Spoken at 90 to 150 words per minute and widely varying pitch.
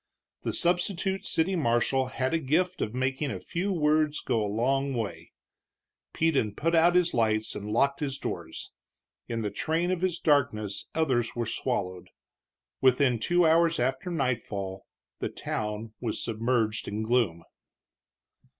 Yes: average, 145 wpm; wide, 6.6 semitones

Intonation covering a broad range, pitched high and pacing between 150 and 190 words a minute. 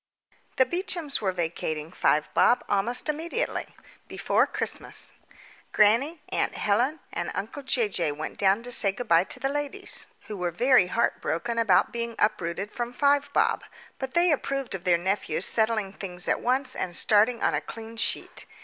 Yes: wide, 5.7 semitones; high, 225 Hz; average, 165 wpm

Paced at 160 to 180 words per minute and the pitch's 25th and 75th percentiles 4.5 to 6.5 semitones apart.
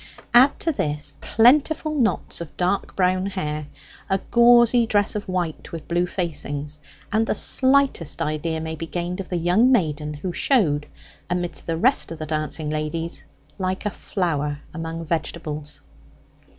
No: average, 150 wpm; average, 5.2 semitones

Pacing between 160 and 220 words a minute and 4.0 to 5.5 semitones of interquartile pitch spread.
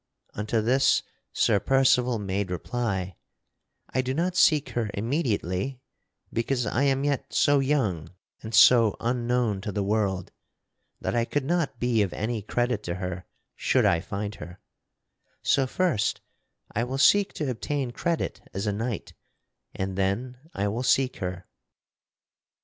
No: average, 145 wpm; average, 5.0 semitones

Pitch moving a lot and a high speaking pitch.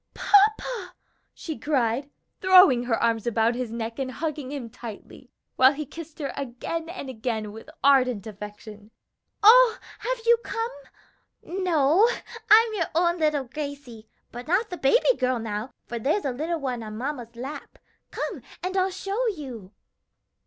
Yes: wide, 7.3 semitones; very high, 280 Hz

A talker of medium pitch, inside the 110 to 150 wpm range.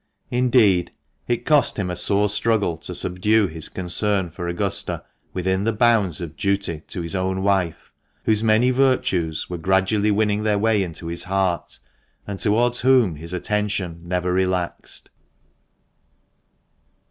No: very low, 95 Hz; average, 140 wpm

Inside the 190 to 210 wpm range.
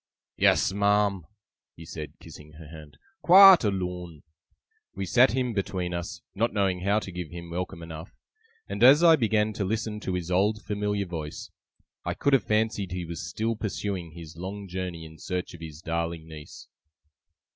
No: average, 170 wpm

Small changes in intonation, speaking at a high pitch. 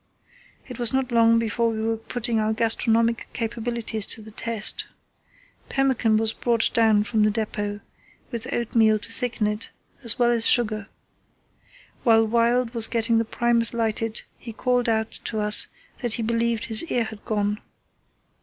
Yes: narrow, 1.4 semitones; high, 230 Hz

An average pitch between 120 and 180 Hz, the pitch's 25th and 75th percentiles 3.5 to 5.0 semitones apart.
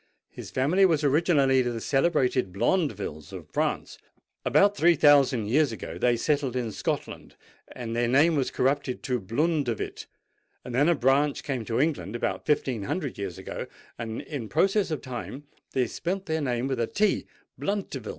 Yes: low, 135 Hz; average, 4.6 semitones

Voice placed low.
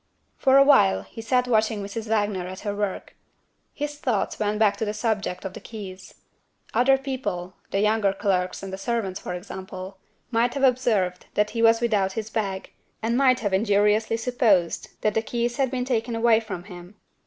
No: high, 215 Hz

